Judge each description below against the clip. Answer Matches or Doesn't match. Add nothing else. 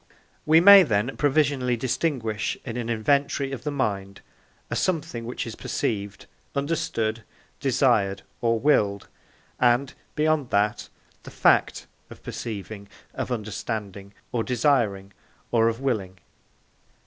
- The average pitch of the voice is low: Matches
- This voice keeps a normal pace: Doesn't match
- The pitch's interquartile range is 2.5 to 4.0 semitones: Doesn't match